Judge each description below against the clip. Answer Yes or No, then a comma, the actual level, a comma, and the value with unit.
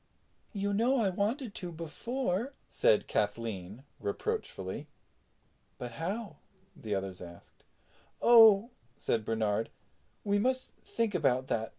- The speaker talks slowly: Yes, slow, 110 wpm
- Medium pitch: Yes, medium, 170 Hz